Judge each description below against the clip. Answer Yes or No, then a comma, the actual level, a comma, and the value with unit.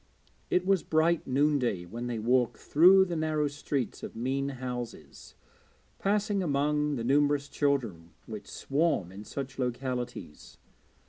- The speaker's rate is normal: No, slow, 130 wpm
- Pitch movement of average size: Yes, average, 3.9 semitones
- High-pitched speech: No, medium, 140 Hz